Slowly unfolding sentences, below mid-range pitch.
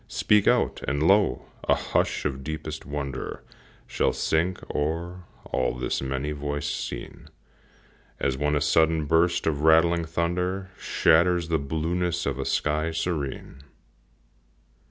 Yes: slow, 130 wpm; very low, 80 Hz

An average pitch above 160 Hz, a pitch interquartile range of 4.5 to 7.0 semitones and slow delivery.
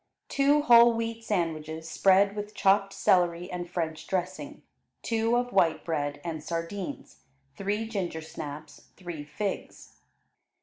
Yes: medium, 185 Hz; average, 5.3 semitones; slow, 120 wpm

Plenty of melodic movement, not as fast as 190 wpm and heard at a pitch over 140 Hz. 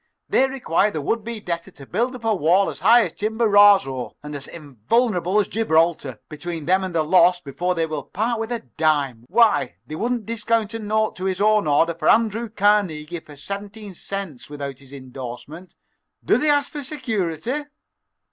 Yes: wide, 6.3 semitones; average, 180 wpm; high, 190 Hz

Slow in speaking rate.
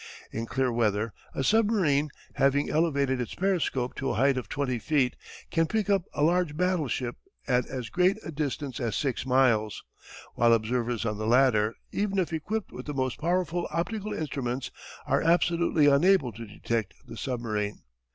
No: average, 165 wpm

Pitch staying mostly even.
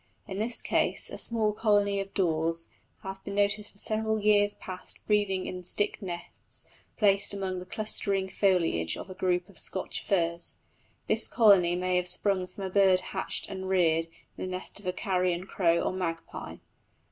Yes: narrow, 2.1 semitones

